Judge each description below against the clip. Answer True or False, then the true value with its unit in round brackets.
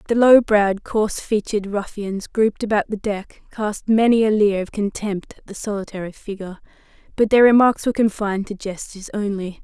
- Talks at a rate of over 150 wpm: True (175 wpm)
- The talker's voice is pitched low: False (205 Hz)